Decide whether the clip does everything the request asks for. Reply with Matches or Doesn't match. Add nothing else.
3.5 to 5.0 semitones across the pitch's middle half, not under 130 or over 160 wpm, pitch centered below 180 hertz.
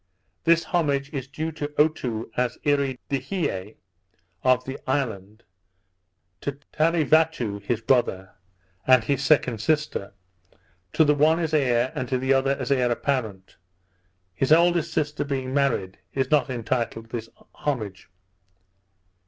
Matches